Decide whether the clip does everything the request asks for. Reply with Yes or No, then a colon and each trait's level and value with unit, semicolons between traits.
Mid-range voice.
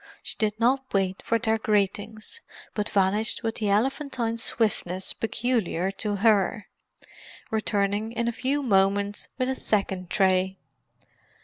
No: high, 215 Hz